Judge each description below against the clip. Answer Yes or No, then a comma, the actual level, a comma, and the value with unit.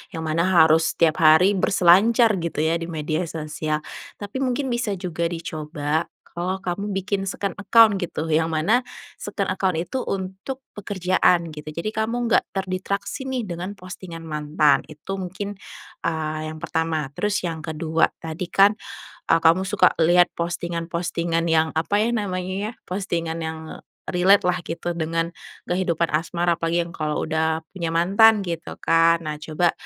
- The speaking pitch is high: No, medium, 170 Hz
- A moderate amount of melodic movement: Yes, average, 3.2 semitones